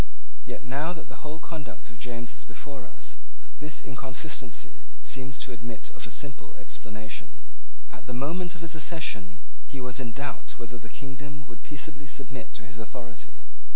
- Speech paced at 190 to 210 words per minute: No, average, 170 wpm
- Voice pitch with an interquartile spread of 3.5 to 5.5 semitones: Yes, average, 3.9 semitones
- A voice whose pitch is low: Yes, low, 130 Hz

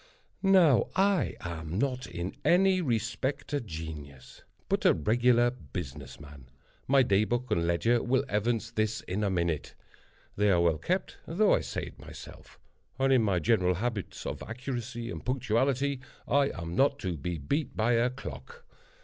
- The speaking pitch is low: Yes, low, 115 Hz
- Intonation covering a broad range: Yes, wide, 7.1 semitones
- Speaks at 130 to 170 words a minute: Yes, average, 165 wpm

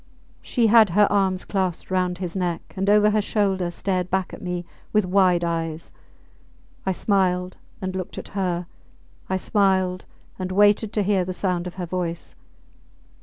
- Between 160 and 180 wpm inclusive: Yes, average, 165 wpm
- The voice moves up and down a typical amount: No, narrow, 1.9 semitones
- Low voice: No, medium, 185 Hz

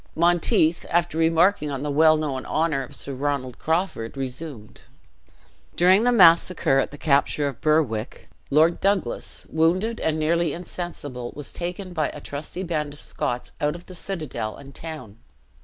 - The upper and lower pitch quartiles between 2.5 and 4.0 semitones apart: Yes, average, 3.6 semitones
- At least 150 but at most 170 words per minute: Yes, average, 155 wpm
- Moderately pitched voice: Yes, medium, 155 Hz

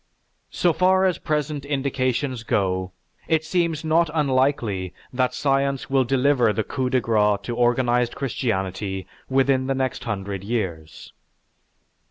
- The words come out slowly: Yes, slow, 130 wpm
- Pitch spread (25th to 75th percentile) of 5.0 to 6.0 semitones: No, average, 4.5 semitones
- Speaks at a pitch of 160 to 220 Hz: No, low, 130 Hz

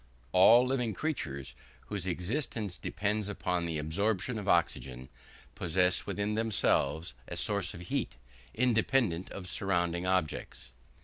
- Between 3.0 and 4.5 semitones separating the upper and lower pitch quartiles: Yes, average, 4.0 semitones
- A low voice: Yes, very low, 95 Hz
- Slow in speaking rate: Yes, slow, 120 wpm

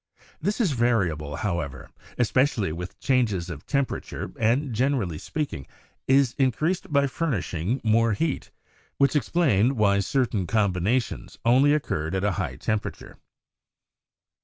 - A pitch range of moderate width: No, wide, 6.5 semitones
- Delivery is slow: Yes, slow, 130 wpm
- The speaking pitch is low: Yes, low, 115 Hz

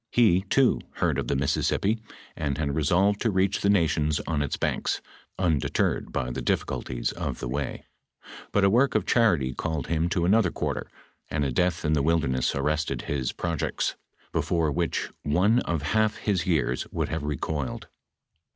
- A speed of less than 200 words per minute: Yes, average, 170 wpm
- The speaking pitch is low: Yes, very low, 80 Hz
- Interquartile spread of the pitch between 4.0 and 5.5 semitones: Yes, average, 4.8 semitones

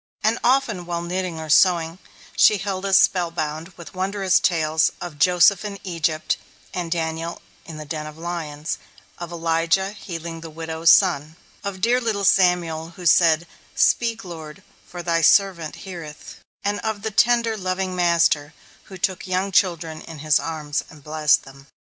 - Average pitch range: Yes, average, 3.0 semitones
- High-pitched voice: No, medium, 170 Hz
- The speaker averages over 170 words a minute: No, average, 160 wpm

